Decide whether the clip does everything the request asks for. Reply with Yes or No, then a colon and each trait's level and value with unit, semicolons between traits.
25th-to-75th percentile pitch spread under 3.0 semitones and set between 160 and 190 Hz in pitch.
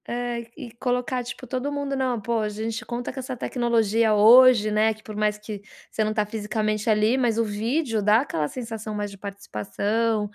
No: narrow, 2.5 semitones; high, 225 Hz